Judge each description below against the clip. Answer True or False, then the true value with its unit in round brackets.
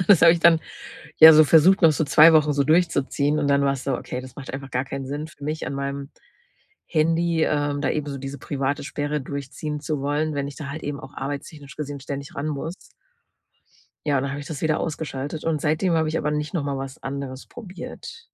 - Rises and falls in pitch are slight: True (2.2 semitones)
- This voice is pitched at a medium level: True (145 Hz)